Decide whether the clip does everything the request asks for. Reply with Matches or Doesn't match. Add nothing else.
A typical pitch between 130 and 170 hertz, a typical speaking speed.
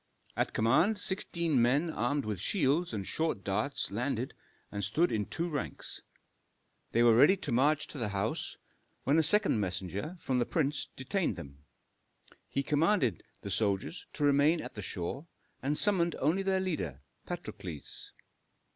Matches